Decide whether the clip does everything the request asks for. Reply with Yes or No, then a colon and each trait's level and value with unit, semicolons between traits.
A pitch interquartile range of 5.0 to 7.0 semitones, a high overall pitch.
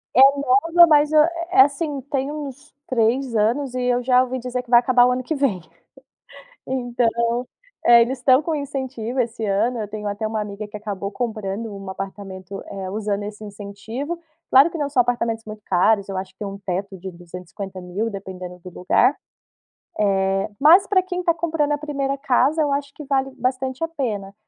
Yes: average, 5.3 semitones; high, 240 Hz